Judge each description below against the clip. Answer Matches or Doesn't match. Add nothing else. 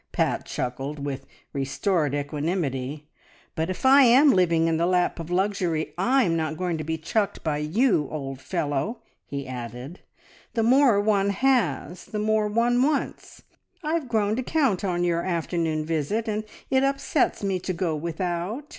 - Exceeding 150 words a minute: Matches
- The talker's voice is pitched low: Doesn't match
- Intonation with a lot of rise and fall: Matches